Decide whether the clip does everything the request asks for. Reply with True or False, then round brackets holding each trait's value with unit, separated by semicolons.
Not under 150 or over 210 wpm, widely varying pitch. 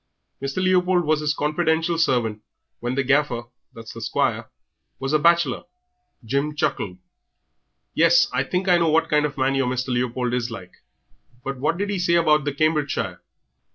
False (170 wpm; 4.8 semitones)